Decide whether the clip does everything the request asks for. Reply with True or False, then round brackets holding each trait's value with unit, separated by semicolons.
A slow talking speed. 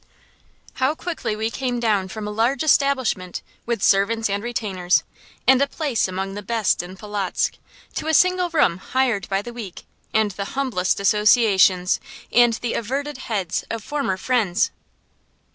False (155 wpm)